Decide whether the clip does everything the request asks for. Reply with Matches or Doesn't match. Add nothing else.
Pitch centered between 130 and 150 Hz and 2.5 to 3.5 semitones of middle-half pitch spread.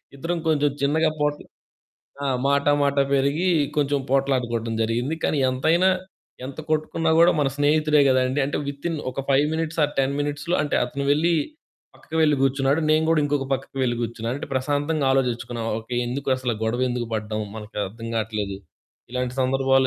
Matches